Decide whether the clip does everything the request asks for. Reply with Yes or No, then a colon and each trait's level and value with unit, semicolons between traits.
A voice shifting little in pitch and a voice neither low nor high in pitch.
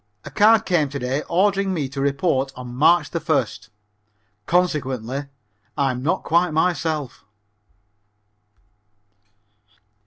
No: average, 4.6 semitones; medium, 150 Hz